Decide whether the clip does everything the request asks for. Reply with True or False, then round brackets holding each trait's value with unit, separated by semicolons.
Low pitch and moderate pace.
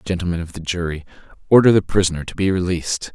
True (90 Hz; 190 wpm)